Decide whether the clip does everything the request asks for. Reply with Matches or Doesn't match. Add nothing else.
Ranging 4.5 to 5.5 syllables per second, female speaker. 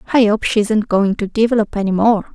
Doesn't match